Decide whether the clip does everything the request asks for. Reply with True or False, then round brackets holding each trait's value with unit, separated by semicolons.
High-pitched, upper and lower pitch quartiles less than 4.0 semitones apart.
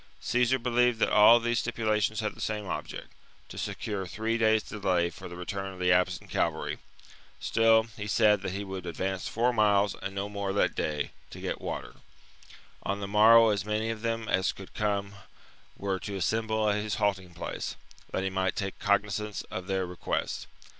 False (105 Hz; 2.4 semitones)